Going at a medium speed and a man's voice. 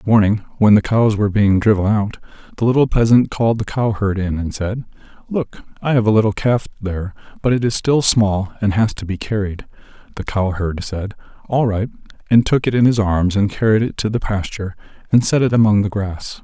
No: fast, 220 wpm; male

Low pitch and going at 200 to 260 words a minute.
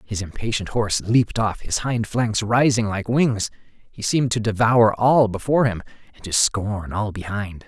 No: low, 110 Hz; average, 170 wpm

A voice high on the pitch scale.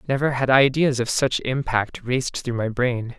No: low, 125 Hz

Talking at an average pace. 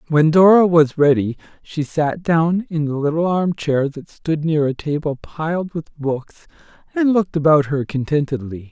Yes: average, 165 wpm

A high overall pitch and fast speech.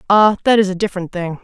Yes: high, 195 Hz; fast, 250 wpm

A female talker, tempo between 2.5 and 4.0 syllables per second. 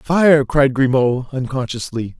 No: male; 3.8 syllables/s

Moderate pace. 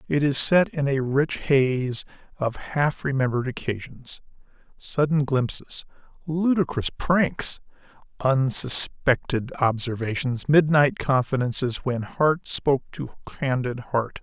No: slow, 105 wpm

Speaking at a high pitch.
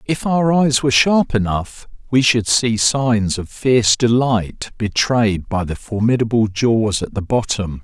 No: low, 115 Hz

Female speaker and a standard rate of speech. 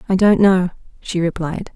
Yes: female; average, 170 wpm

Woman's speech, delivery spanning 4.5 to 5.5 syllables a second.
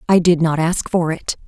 Yes: female; 4.8 syllables/s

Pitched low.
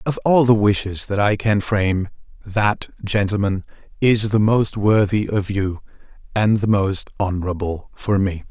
Yes: low, 100 Hz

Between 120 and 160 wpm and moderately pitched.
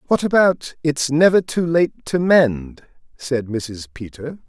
Yes: average, 145 wpm; medium, 145 Hz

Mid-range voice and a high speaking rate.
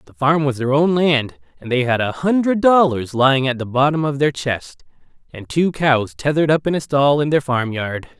Yes: medium, 145 Hz; fast, 225 wpm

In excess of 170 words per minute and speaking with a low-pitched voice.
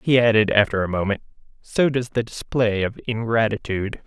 No: average, 160 wpm; low, 110 Hz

